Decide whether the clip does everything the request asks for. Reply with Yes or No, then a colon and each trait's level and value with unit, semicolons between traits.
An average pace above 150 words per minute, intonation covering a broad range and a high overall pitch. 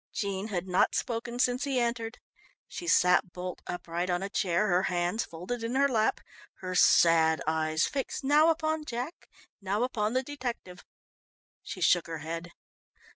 Yes: average, 160 wpm; wide, 5.8 semitones; high, 200 Hz